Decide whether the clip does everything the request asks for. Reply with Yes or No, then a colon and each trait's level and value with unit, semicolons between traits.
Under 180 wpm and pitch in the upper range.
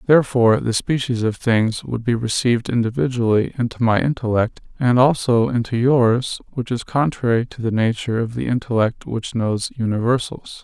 No: average, 160 wpm; low, 120 Hz